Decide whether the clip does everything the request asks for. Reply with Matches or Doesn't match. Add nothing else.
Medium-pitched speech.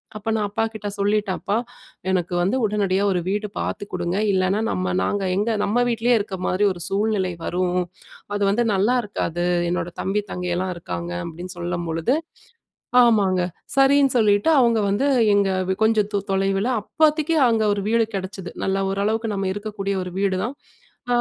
Doesn't match